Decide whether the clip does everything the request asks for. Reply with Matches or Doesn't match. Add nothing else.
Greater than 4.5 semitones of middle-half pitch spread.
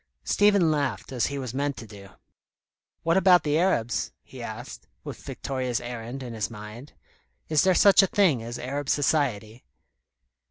Matches